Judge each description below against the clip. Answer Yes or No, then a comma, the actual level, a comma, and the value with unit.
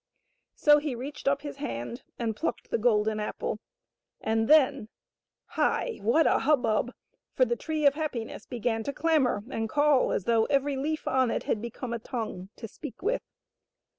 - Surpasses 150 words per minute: Yes, average, 175 wpm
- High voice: Yes, very high, 255 Hz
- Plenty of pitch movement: No, average, 4.5 semitones